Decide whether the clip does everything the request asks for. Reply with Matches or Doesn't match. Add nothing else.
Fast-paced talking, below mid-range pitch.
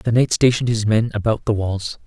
Matches